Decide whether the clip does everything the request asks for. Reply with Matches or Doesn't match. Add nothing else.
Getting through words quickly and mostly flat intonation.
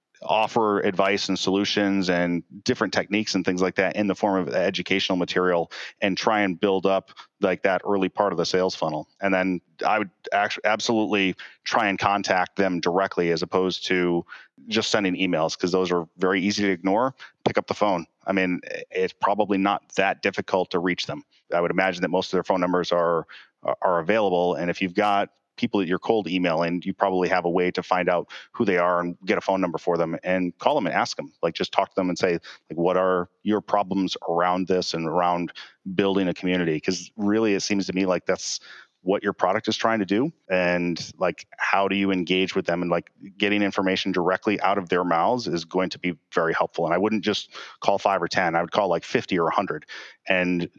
Matches